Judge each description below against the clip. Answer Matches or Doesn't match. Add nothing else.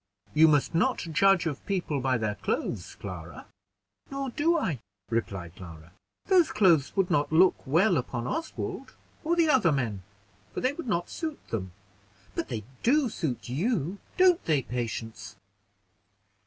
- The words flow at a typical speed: Matches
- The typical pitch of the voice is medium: Matches